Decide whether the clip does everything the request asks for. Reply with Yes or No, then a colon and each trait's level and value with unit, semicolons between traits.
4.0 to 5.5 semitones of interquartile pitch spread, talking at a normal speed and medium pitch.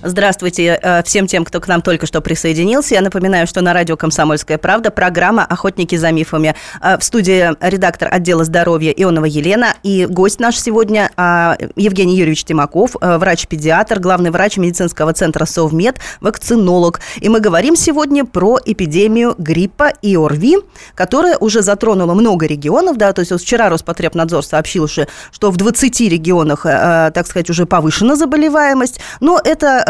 Yes: average, 4.4 semitones; average, 145 wpm; medium, 180 Hz